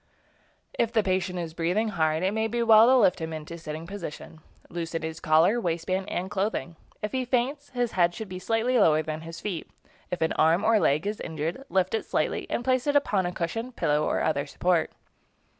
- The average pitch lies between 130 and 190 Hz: Yes, medium, 185 Hz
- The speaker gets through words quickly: Yes, fast, 215 wpm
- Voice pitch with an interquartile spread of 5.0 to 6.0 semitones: Yes, wide, 5.5 semitones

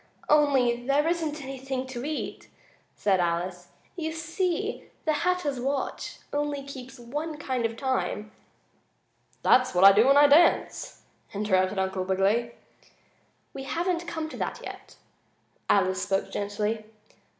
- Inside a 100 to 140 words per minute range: Yes, slow, 135 wpm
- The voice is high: Yes, very high, 260 Hz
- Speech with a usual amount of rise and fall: No, wide, 6.4 semitones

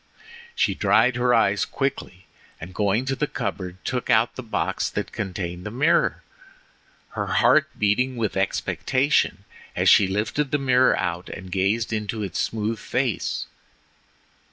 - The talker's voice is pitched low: Yes, low, 110 Hz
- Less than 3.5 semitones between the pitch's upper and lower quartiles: No, average, 4.9 semitones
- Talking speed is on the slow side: No, average, 145 wpm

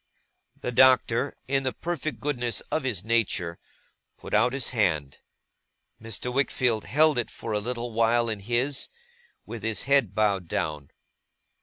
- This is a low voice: Yes, low, 120 Hz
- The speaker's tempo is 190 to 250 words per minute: No, average, 145 wpm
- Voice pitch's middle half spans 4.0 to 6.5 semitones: No, average, 3.5 semitones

